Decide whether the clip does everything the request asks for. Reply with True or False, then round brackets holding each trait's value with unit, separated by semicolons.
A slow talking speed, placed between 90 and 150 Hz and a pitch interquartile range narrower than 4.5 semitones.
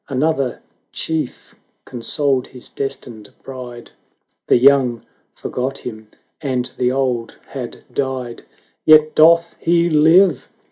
True (105 wpm; 135 Hz; 3.9 semitones)